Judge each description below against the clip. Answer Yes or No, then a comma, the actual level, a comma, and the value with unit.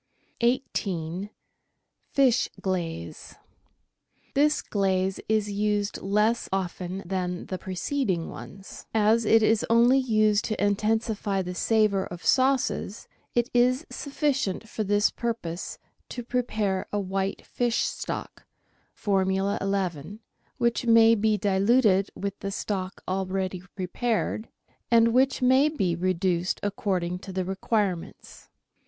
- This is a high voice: Yes, high, 205 Hz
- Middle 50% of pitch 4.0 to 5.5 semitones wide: No, average, 3.5 semitones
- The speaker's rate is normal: No, slow, 115 wpm